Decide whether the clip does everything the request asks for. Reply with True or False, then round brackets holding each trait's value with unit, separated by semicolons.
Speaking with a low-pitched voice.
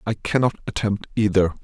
True (105 Hz)